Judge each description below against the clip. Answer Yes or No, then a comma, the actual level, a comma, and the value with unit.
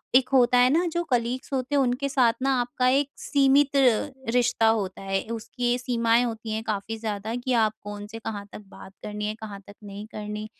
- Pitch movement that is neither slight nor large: Yes, average, 3.1 semitones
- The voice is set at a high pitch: Yes, high, 230 Hz